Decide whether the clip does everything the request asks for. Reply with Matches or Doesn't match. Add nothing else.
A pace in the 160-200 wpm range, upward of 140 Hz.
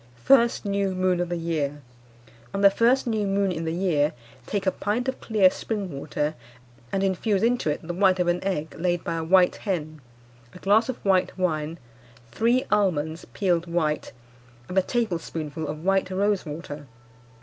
Matches